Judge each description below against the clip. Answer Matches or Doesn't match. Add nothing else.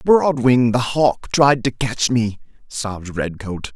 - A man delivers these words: Matches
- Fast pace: Doesn't match